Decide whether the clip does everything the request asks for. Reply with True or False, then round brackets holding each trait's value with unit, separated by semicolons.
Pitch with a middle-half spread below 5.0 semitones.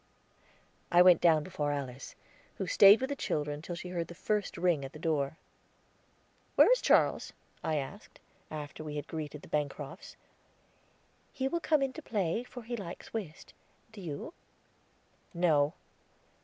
False (5.6 semitones)